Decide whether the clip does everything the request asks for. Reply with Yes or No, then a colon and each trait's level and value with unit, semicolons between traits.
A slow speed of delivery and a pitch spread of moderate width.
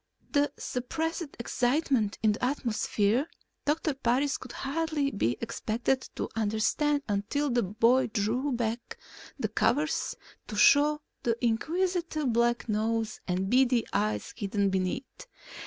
Yes: slow, 125 wpm; average, 4.9 semitones